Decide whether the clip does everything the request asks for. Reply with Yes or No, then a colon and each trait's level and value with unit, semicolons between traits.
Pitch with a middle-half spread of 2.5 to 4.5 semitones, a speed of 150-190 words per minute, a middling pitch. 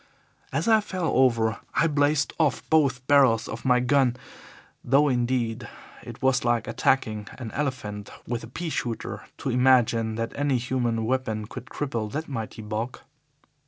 No: average, 3.4 semitones; average, 155 wpm; low, 125 Hz